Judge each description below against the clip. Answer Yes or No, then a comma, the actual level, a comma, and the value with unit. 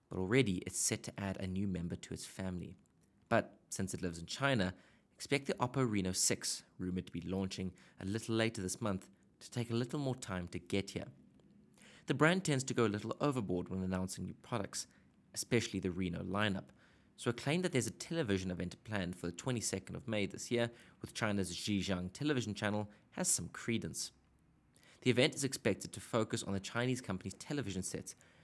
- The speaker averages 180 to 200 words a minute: Yes, average, 195 wpm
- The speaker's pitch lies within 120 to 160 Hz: No, low, 100 Hz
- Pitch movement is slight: No, average, 4.5 semitones